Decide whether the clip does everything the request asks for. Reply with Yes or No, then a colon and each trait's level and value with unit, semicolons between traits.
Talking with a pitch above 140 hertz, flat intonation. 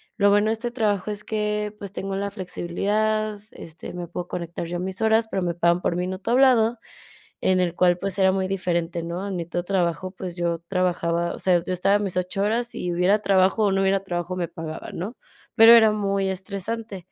No: high, 190 Hz; average, 3.1 semitones